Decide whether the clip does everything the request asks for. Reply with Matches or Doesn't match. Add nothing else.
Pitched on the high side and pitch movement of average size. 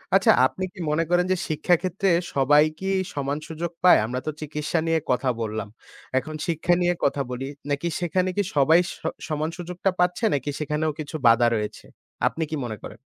Doesn't match